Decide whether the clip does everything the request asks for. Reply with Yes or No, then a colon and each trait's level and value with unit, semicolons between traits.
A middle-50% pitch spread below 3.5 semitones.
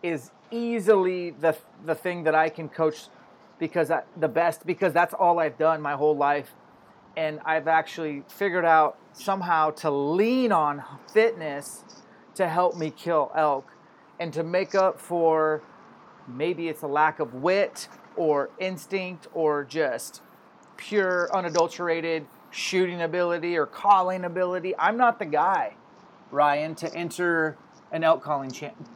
Yes: average, 2.9 semitones